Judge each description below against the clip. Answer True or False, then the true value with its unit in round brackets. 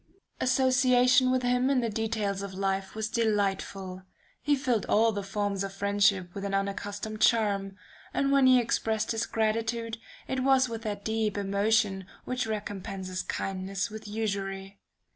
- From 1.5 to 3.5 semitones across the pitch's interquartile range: True (2.9 semitones)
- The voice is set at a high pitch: True (215 Hz)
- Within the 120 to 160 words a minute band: True (150 wpm)